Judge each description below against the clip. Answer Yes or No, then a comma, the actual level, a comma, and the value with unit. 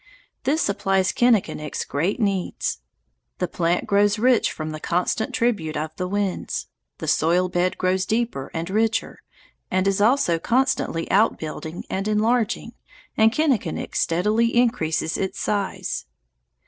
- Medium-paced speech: No, slow, 130 wpm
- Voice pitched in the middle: No, high, 195 Hz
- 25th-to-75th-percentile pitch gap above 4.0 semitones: Yes, average, 4.7 semitones